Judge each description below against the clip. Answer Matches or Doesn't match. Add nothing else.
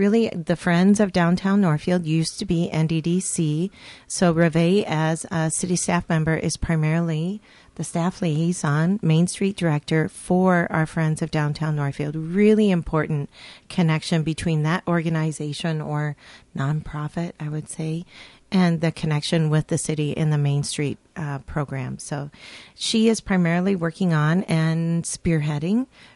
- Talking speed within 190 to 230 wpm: Doesn't match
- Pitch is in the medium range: Matches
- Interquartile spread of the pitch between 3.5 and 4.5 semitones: Doesn't match